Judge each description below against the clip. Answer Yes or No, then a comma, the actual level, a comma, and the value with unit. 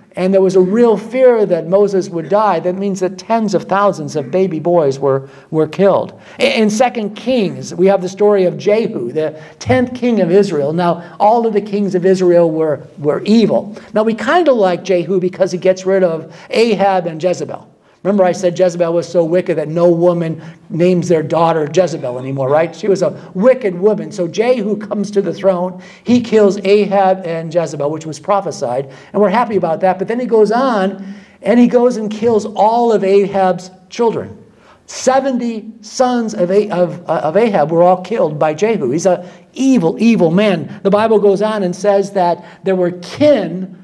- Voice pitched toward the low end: No, high, 190 Hz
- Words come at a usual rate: Yes, average, 190 wpm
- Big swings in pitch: No, average, 3.4 semitones